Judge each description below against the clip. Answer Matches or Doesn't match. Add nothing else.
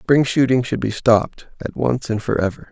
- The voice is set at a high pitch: Doesn't match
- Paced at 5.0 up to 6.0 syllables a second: Matches